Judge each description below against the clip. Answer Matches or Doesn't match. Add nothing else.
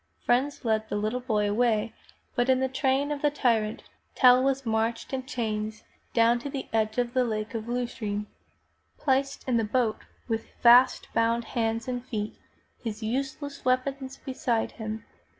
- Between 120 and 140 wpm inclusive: Doesn't match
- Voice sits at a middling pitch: Doesn't match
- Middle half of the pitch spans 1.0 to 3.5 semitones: Matches